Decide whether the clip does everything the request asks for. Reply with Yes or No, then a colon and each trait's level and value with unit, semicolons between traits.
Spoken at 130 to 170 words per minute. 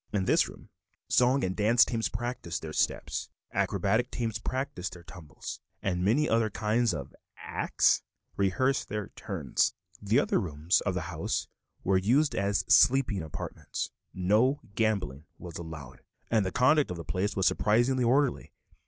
Yes: average, 155 wpm